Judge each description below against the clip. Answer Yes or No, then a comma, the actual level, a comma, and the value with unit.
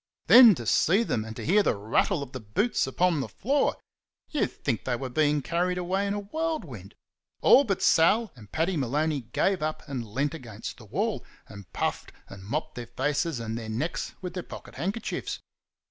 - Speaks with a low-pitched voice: No, medium, 155 Hz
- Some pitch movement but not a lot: No, wide, 8.3 semitones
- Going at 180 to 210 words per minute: Yes, average, 190 wpm